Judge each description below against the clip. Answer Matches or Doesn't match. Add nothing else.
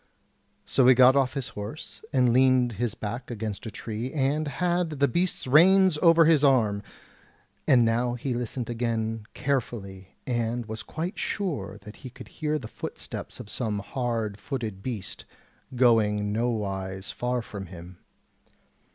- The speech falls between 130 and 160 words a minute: Matches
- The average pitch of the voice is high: Doesn't match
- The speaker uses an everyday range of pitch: Matches